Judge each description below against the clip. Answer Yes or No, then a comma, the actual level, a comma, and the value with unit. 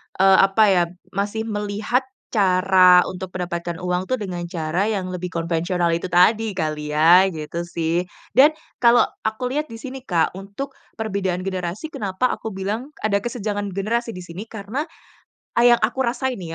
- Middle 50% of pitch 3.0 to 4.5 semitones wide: Yes, average, 3.8 semitones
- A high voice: Yes, high, 195 Hz